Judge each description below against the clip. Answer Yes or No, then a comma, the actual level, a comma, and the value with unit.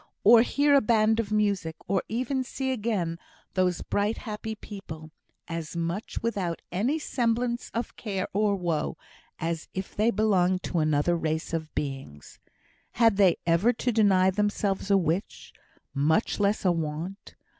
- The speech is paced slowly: No, average, 150 wpm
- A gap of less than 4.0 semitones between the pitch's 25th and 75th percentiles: No, average, 4.8 semitones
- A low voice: No, high, 195 Hz